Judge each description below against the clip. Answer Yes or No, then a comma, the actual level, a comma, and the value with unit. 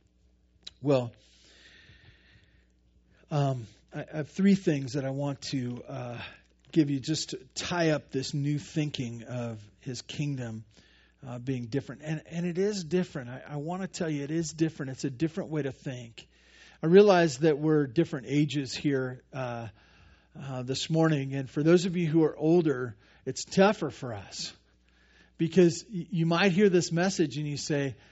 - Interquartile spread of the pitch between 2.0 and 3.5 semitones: No, average, 4.9 semitones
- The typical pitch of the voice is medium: Yes, medium, 145 Hz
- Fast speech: No, average, 165 wpm